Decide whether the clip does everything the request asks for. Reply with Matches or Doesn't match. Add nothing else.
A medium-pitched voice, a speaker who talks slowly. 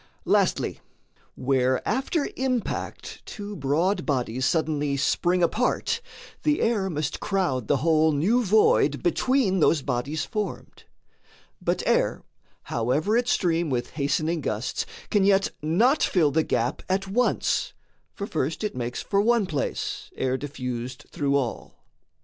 Matches